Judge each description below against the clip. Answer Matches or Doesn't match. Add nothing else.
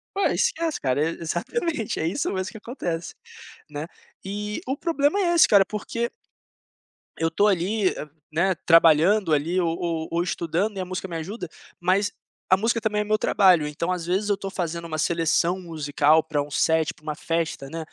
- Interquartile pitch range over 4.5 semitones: Doesn't match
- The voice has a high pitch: Doesn't match